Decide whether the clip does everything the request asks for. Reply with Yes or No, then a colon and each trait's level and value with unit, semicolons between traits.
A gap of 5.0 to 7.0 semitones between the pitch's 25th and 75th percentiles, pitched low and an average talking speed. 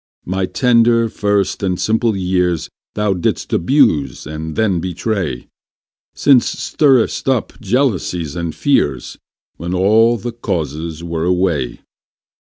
No: wide, 5.5 semitones; very low, 95 Hz; slow, 115 wpm